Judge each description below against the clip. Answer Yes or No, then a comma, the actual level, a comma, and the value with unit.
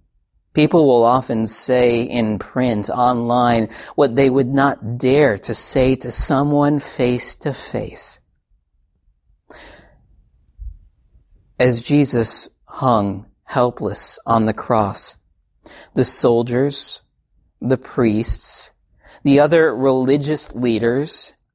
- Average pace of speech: No, slow, 95 wpm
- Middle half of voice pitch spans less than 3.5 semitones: No, average, 4.2 semitones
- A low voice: Yes, low, 120 Hz